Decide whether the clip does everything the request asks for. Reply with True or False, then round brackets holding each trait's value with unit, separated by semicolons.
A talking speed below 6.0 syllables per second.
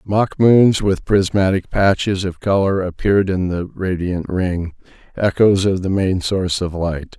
True (4.2 syllables/s)